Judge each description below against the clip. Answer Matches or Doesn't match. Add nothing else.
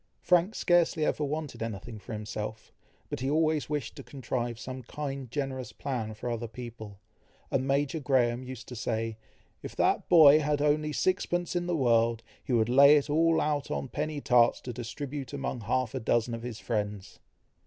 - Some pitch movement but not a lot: Matches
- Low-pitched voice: Matches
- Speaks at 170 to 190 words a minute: Matches